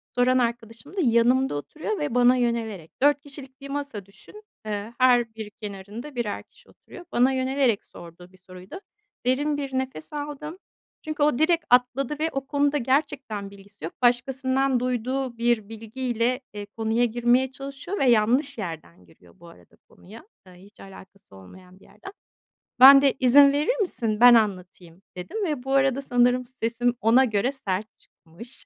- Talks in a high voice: Yes, high, 245 Hz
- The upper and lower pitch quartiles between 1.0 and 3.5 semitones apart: No, average, 4.5 semitones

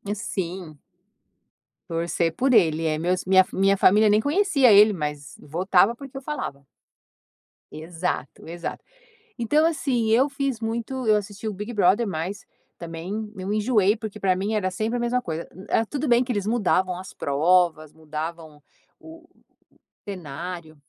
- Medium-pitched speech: No, high, 195 Hz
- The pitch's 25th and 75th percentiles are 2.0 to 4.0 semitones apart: No, wide, 5.6 semitones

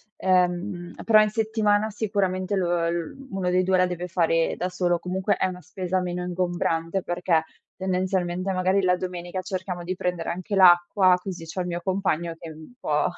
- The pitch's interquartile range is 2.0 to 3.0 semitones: No, narrow, 1.4 semitones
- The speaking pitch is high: No, medium, 180 Hz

